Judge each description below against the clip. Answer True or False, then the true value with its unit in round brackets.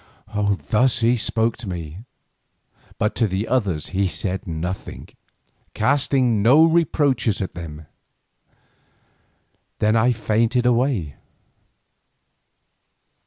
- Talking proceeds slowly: True (95 wpm)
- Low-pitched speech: True (110 Hz)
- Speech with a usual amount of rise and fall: True (4.7 semitones)